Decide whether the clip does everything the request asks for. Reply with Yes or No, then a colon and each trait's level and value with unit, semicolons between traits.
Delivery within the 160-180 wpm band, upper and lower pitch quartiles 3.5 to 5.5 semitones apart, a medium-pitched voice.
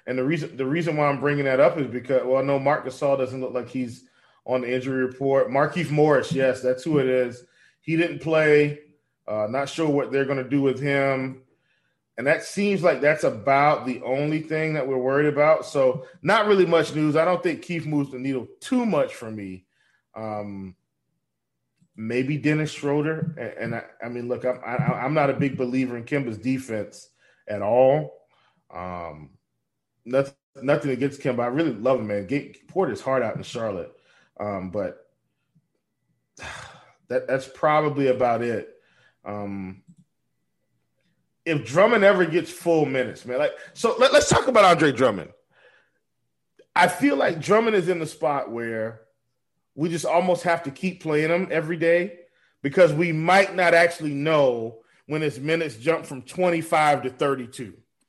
Yes: average, 175 wpm; average, 4.3 semitones; medium, 145 Hz